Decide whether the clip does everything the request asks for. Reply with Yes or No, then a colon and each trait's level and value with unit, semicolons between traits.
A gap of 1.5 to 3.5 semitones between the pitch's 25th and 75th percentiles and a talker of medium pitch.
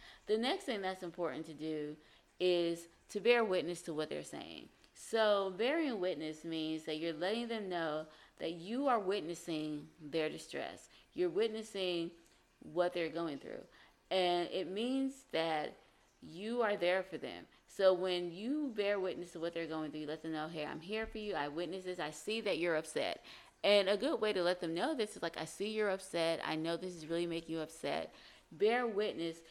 No: average, 4.3 semitones; medium, 175 Hz